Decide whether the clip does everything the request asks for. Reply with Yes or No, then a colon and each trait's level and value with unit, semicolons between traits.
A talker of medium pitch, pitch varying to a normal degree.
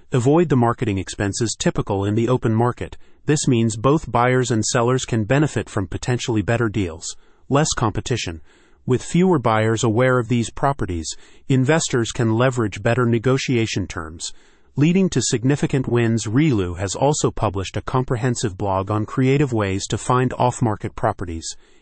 No: low, 120 Hz; average, 3.6 semitones